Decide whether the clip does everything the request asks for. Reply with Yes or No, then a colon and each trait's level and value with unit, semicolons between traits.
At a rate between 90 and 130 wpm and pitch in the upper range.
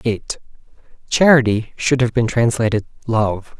No: slow, 115 wpm; low, 115 Hz